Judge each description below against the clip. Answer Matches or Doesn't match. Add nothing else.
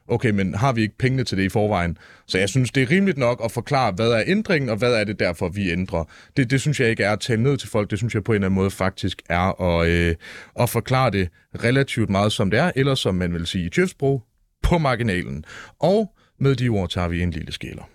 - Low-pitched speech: Matches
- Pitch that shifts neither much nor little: Doesn't match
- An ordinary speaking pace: Doesn't match